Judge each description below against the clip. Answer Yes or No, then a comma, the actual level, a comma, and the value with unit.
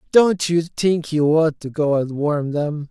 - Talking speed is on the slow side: No, fast, 205 wpm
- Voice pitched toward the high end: No, medium, 155 Hz